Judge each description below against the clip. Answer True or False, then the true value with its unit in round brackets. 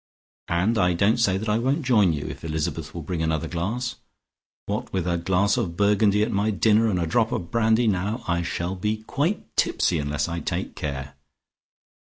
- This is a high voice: False (95 Hz)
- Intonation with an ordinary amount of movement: True (4.6 semitones)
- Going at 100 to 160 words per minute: False (195 wpm)